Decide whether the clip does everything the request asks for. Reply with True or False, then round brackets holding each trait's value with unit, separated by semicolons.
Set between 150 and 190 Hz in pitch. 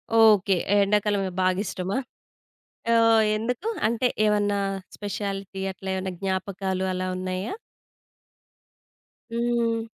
False (200 Hz)